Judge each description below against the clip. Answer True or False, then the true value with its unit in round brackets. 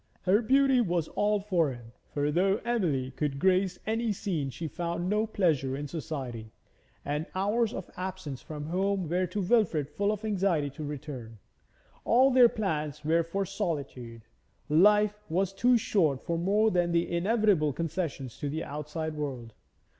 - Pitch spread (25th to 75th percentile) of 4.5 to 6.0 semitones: True (5.4 semitones)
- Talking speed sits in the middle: True (160 wpm)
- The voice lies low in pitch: False (170 Hz)